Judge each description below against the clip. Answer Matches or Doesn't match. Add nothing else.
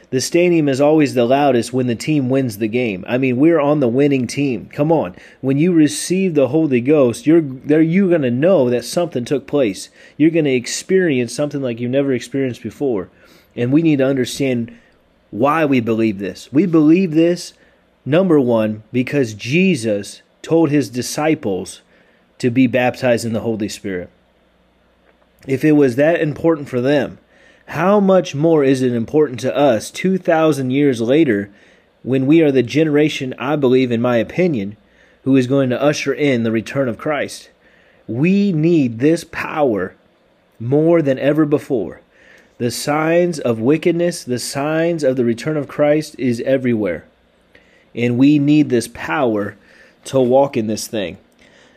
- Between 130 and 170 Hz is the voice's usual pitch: Matches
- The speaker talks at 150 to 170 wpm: Matches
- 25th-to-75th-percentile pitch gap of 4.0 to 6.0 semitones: Matches